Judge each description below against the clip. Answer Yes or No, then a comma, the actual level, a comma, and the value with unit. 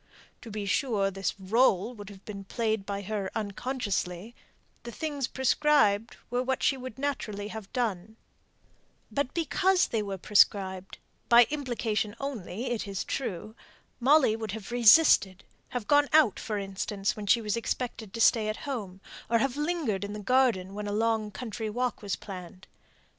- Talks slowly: No, average, 165 wpm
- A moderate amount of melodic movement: Yes, average, 3.9 semitones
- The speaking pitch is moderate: No, high, 220 Hz